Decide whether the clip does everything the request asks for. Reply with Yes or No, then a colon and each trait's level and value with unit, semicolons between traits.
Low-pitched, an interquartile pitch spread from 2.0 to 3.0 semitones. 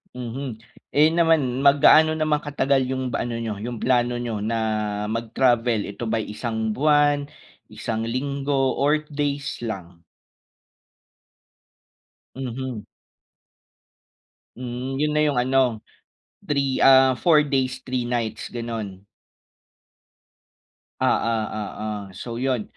No: low, 125 Hz; average, 3.5 semitones